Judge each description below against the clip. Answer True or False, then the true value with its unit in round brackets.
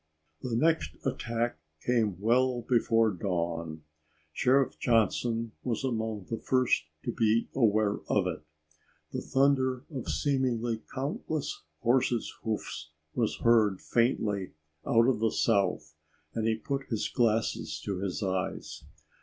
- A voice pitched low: True (115 Hz)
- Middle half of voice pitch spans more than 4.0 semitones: False (3.5 semitones)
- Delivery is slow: True (125 wpm)